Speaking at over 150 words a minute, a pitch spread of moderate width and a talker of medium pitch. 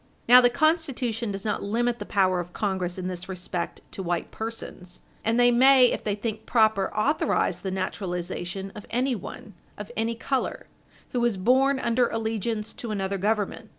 No: average, 170 wpm; average, 3.9 semitones; high, 220 Hz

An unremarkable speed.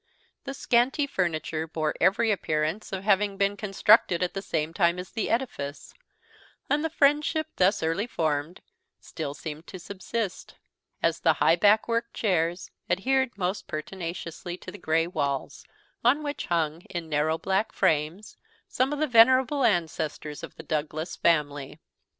Yes: average, 150 wpm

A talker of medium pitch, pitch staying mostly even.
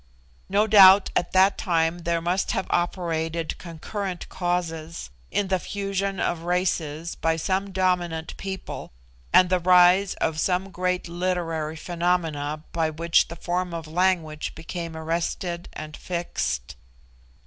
Yes: medium, 175 Hz; narrow, 2.2 semitones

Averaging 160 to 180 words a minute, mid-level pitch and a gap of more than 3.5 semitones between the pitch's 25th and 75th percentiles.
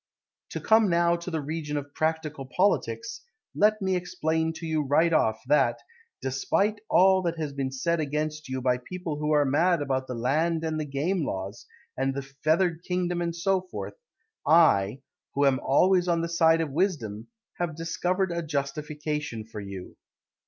Yes: average, 175 wpm; medium, 155 Hz; average, 4.0 semitones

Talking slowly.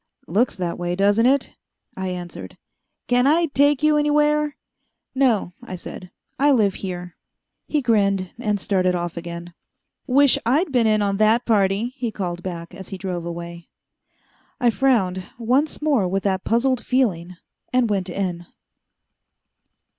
No: average, 145 wpm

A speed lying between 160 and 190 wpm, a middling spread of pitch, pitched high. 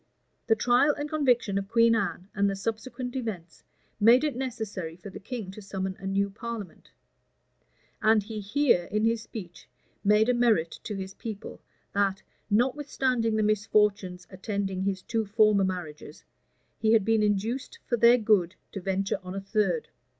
Yes: average, 165 wpm; average, 3.2 semitones; high, 210 Hz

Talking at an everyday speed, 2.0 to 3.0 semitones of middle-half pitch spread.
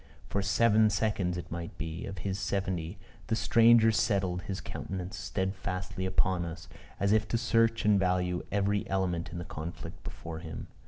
Yes: average, 165 wpm; average, 2.7 semitones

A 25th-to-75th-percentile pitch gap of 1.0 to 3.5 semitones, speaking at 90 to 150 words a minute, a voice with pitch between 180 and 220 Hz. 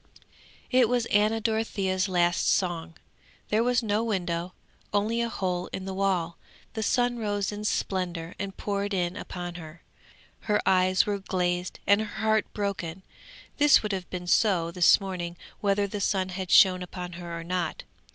No: average, 2.8 semitones; average, 165 wpm; high, 190 Hz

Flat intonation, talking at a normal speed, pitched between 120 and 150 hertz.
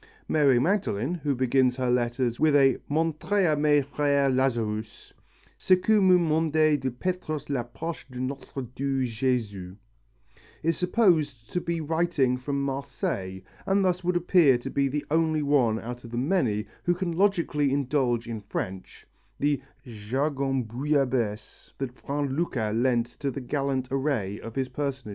No: average, 4.1 semitones; average, 155 wpm; low, 135 Hz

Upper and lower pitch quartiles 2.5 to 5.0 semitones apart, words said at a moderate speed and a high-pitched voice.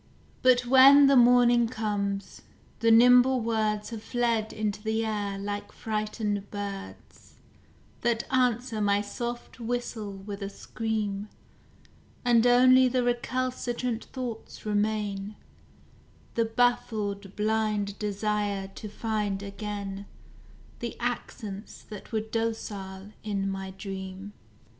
No: average, 2.9 semitones; slow, 110 wpm; high, 215 Hz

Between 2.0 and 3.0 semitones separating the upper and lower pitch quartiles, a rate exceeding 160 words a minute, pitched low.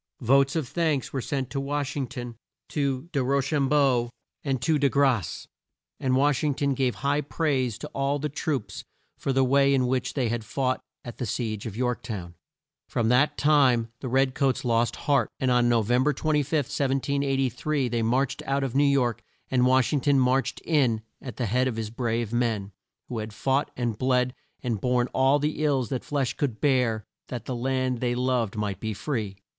Yes: narrow, 2.6 semitones; average, 200 wpm; low, 130 Hz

